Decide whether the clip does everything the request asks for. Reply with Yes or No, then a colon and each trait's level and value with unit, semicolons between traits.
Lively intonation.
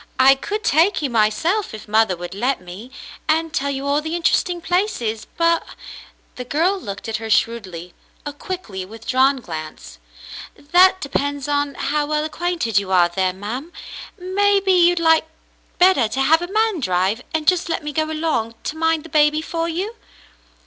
Yes: wide, 7.1 semitones